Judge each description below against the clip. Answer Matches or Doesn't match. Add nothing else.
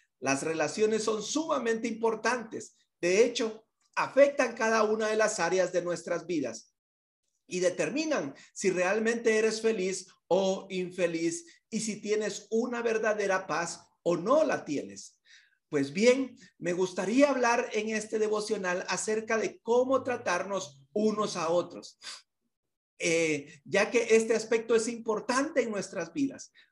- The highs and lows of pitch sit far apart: Doesn't match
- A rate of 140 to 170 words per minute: Doesn't match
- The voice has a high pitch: Matches